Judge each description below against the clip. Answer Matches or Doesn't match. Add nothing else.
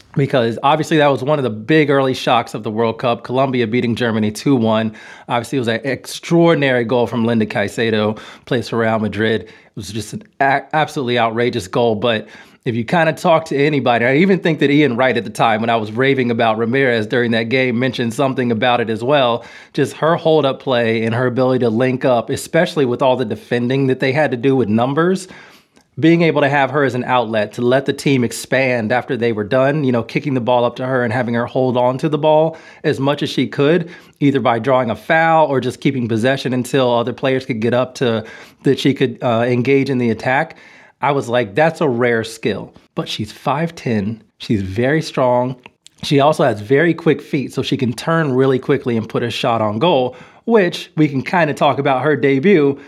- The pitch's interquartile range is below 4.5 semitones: Matches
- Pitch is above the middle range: Doesn't match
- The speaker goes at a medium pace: Doesn't match